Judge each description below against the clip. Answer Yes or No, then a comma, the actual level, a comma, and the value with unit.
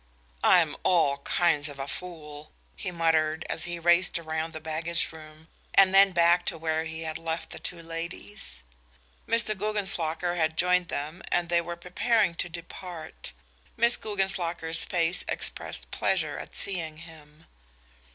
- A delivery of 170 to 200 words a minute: No, average, 150 wpm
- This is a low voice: No, medium, 170 Hz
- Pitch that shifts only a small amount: Yes, narrow, 2.2 semitones